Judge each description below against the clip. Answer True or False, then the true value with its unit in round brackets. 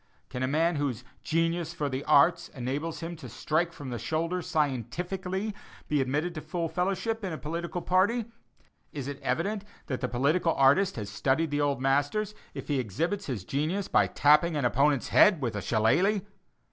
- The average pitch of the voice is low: False (155 Hz)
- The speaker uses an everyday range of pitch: True (4.7 semitones)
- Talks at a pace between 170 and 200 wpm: True (180 wpm)